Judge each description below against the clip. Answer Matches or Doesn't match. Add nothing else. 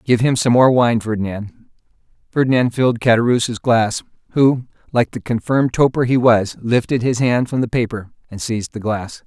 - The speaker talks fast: Doesn't match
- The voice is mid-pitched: Doesn't match